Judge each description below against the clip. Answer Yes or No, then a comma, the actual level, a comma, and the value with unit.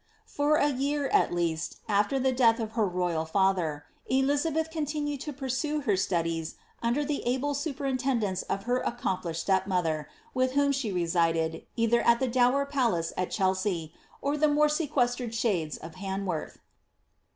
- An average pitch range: No, wide, 7.4 semitones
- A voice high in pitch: Yes, high, 235 Hz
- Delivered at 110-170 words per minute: Yes, average, 165 wpm